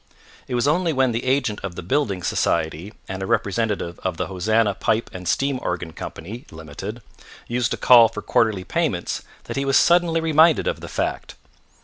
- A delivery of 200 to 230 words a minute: No, average, 180 wpm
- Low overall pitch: Yes, low, 115 Hz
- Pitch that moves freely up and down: Yes, wide, 6.5 semitones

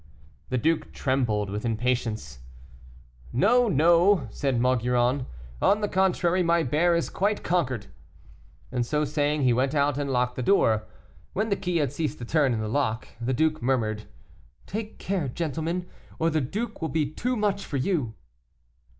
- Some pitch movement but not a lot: No, wide, 5.9 semitones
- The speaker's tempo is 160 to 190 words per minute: Yes, average, 165 wpm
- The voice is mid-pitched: Yes, medium, 145 Hz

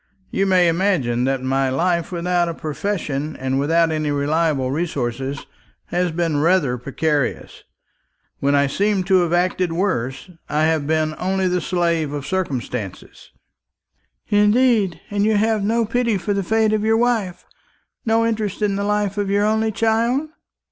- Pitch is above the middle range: No, medium, 175 Hz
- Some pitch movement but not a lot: No, wide, 5.7 semitones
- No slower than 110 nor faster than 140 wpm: No, average, 155 wpm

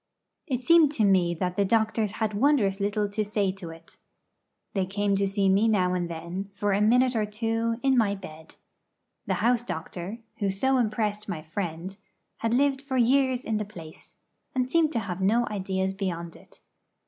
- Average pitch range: Yes, average, 3.4 semitones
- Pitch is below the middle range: No, high, 205 Hz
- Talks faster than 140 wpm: Yes, average, 185 wpm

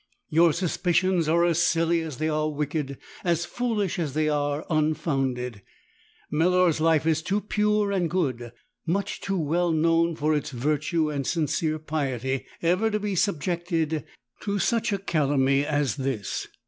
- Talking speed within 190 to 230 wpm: No, average, 150 wpm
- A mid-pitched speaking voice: Yes, medium, 160 Hz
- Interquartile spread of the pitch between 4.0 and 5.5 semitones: No, average, 3.2 semitones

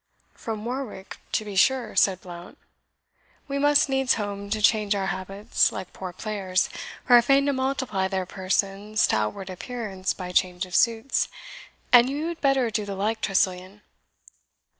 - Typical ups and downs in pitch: Yes, average, 4.6 semitones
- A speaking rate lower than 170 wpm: Yes, average, 160 wpm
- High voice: Yes, high, 210 Hz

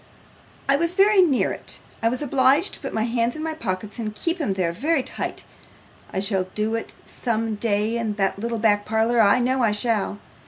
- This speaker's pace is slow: No, fast, 205 wpm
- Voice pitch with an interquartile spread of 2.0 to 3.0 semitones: No, average, 4.0 semitones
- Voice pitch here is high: Yes, high, 230 Hz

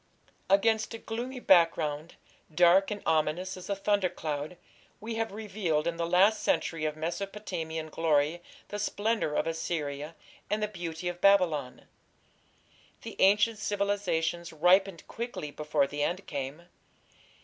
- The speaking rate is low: Yes, slow, 130 wpm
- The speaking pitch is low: No, medium, 175 Hz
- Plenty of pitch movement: No, average, 4.3 semitones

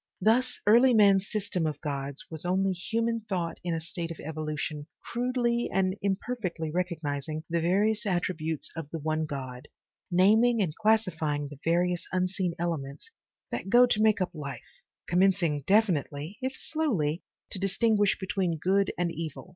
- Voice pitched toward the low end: No, medium, 180 Hz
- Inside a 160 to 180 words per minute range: No, average, 150 wpm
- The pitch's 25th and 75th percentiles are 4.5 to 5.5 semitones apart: Yes, average, 5.0 semitones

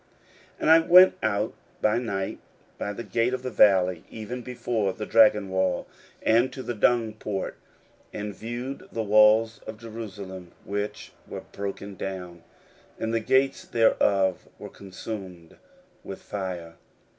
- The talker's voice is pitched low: Yes, low, 105 Hz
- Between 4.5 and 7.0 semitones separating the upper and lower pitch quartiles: No, average, 3.2 semitones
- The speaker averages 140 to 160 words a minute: Yes, average, 145 wpm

